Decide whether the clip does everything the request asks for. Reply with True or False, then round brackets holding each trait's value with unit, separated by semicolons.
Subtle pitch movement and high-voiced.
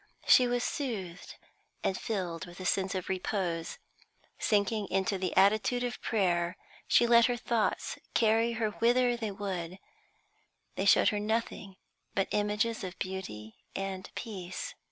False (3.6 semitones; 200 Hz)